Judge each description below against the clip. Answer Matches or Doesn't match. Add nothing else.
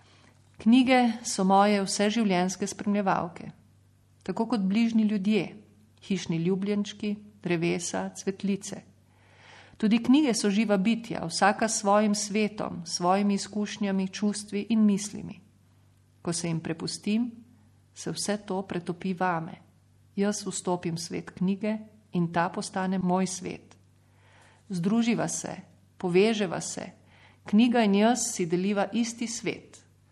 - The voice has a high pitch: Matches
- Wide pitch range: Doesn't match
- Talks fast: Doesn't match